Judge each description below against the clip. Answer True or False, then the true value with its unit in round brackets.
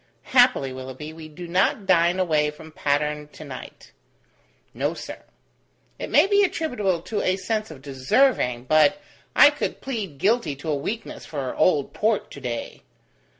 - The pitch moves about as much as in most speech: False (6.9 semitones)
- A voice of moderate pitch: True (165 Hz)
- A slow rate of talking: False (155 wpm)